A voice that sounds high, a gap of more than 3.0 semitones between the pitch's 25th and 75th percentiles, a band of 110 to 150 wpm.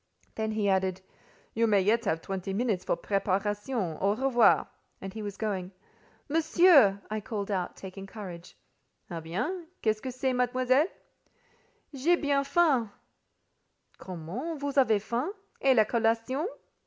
Yes: high, 220 Hz; average, 5.3 semitones; average, 140 wpm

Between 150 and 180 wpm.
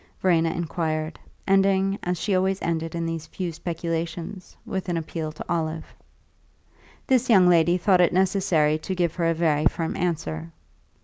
Yes: average, 160 wpm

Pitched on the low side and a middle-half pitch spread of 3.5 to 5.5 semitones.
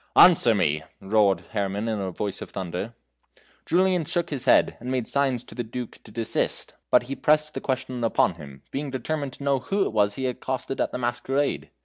Yes: low, 125 Hz; average, 5.1 semitones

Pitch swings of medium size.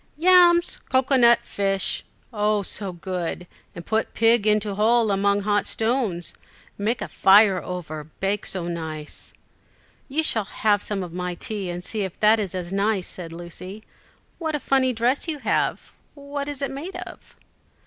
Yes: average, 4.9 semitones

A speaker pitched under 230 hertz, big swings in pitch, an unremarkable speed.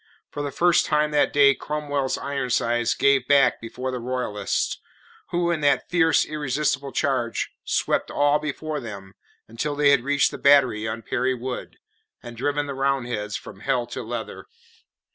No: medium, 140 Hz; average, 3.3 semitones; average, 160 wpm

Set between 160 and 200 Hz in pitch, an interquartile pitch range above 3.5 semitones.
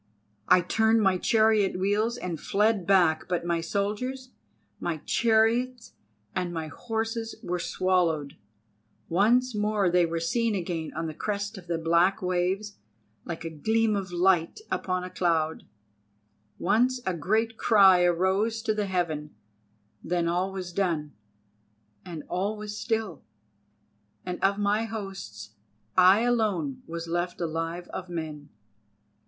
Yes: medium, 185 Hz; average, 4.1 semitones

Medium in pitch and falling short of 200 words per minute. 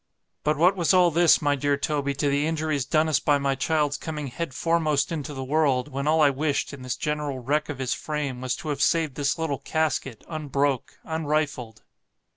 No: medium, 145 Hz; fast, 205 wpm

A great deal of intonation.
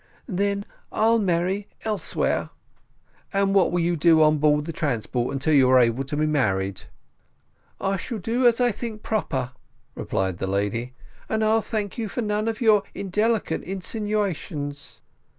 Yes: wide, 7.1 semitones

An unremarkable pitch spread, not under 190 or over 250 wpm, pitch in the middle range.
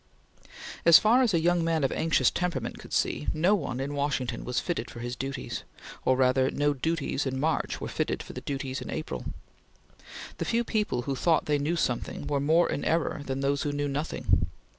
Yes: average, 3.8 semitones; fast, 205 wpm; medium, 145 Hz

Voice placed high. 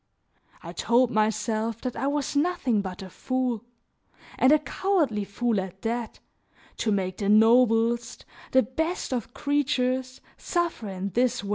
Yes: high, 235 Hz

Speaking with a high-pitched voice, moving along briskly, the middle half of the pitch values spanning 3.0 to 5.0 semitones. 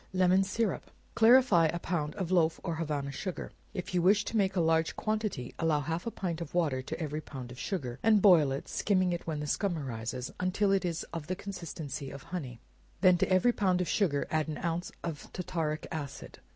No: medium, 170 Hz; fast, 215 wpm; average, 3.9 semitones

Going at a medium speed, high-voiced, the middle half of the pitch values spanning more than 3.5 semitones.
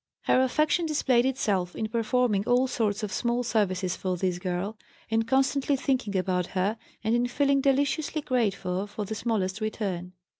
Yes: average, 160 wpm; high, 225 Hz; average, 5.2 semitones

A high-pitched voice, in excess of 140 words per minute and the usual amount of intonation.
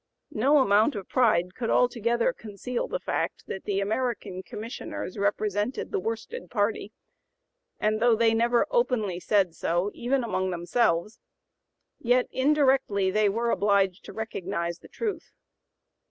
No: high, 215 Hz; slow, 135 wpm; average, 3.7 semitones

